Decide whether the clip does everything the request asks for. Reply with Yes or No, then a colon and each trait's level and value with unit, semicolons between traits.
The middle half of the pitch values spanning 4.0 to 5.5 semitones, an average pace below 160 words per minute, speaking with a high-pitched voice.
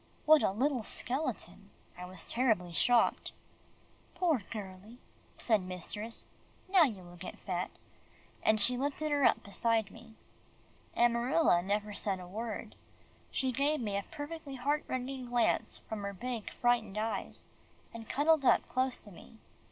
Yes: average, 4.7 semitones; average, 145 wpm; high, 230 Hz